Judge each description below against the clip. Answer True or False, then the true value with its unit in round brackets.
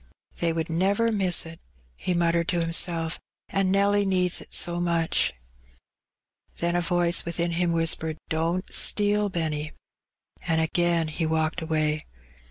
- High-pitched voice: False (170 Hz)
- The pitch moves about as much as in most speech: False (1.9 semitones)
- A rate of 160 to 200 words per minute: False (145 wpm)